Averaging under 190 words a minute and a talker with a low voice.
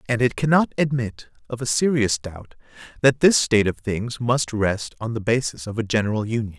No: average, 200 wpm; low, 115 Hz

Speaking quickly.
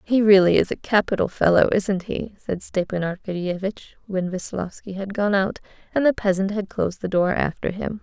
No: average, 185 wpm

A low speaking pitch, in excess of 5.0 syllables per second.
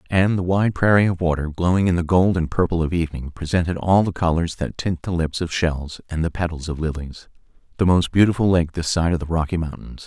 Yes: very low, 85 Hz; 5.9 syllables/s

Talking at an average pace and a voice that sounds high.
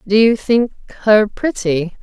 Yes: average, 150 wpm; high, 210 Hz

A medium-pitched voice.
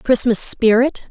No: high, 240 Hz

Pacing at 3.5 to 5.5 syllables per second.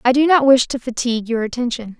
No: 6.4 syllables/s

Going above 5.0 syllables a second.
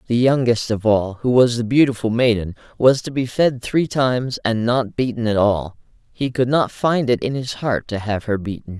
No: 4.9 syllables/s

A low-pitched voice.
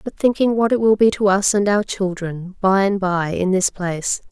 No: high, 195 Hz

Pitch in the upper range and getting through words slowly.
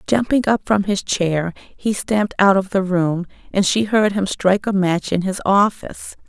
No: high, 195 Hz; average, 200 wpm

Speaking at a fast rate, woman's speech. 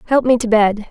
Yes: fast, 265 wpm; female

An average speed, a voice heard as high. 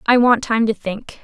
No: fast, 245 wpm; high, 225 Hz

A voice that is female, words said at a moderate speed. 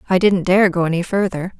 No: female; fast, 225 wpm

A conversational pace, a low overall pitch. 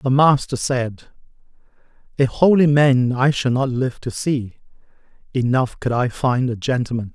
Yes: average, 150 wpm; low, 130 Hz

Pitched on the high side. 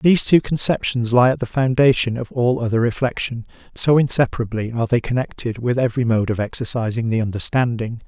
No: low, 120 Hz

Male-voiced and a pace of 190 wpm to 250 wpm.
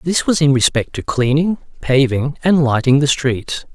No: male; average, 175 wpm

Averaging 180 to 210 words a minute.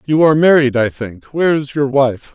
No: fast, 230 wpm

